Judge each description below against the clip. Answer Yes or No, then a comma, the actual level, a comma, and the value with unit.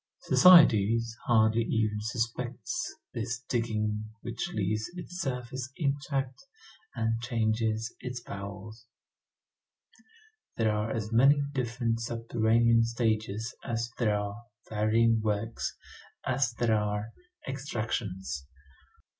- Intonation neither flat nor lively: No, narrow, 2.1 semitones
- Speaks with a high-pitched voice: No, low, 115 Hz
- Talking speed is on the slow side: Yes, slow, 95 wpm